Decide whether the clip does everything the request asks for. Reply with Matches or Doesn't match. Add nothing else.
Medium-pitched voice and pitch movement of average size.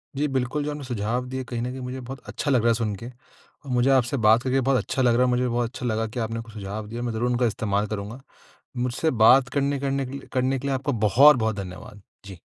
Doesn't match